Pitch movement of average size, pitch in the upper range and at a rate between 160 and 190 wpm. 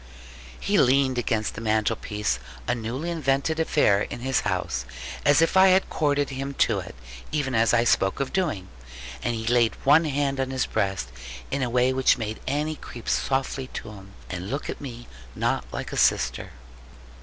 No: average, 4.2 semitones; low, 130 Hz; average, 180 wpm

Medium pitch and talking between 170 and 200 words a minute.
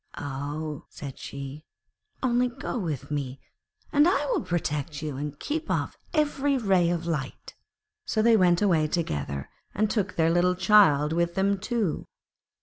No: medium, 170 Hz; average, 150 wpm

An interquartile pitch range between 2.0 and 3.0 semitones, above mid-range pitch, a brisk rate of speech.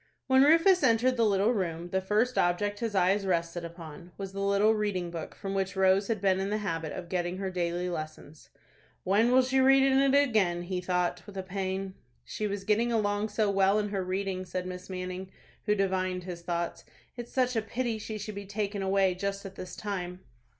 Yes: average, 2.7 semitones; high, 195 Hz; fast, 210 wpm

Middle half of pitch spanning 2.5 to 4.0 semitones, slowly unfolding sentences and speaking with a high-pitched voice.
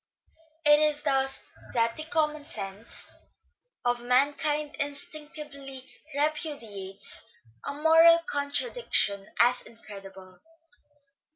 No: average, 4.7 semitones; slow, 85 wpm; very high, 285 Hz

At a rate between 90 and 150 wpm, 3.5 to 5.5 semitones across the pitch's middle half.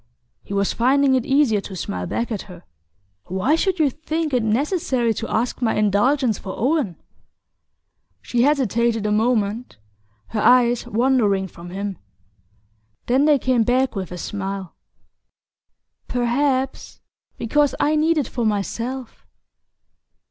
Yes: slow, 135 wpm; average, 4.7 semitones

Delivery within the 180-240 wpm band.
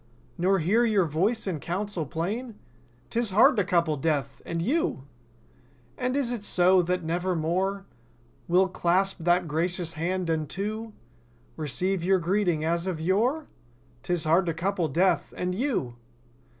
No: average, 140 wpm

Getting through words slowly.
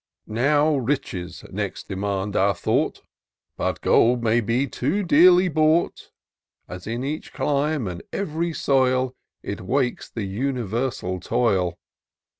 Yes: slow, 125 wpm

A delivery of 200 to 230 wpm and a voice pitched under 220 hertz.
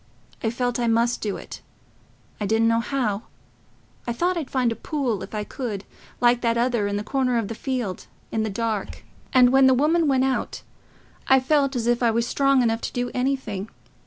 No: fast, 205 wpm; high, 240 Hz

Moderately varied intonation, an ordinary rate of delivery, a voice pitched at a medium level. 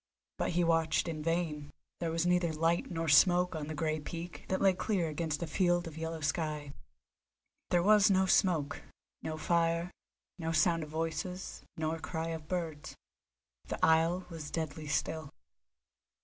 No: narrow, 1.8 semitones; average, 160 wpm; medium, 165 Hz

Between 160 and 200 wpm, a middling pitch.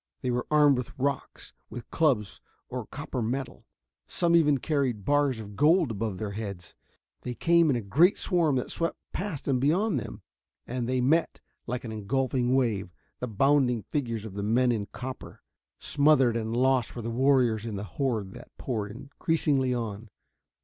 No: average, 170 wpm; low, 125 Hz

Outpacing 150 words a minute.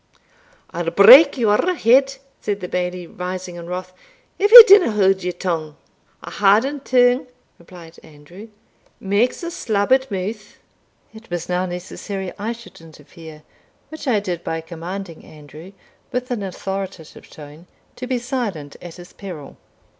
No: average, 145 wpm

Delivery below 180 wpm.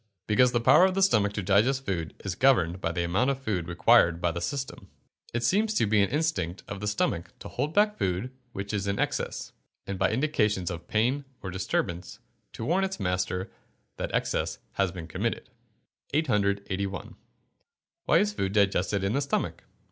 No: average, 185 wpm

